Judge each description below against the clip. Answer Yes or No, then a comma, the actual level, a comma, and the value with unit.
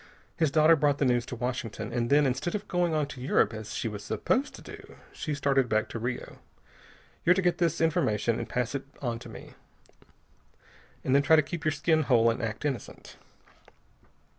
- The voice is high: No, medium, 140 Hz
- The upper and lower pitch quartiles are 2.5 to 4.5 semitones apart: No, average, 5.0 semitones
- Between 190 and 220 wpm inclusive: Yes, average, 195 wpm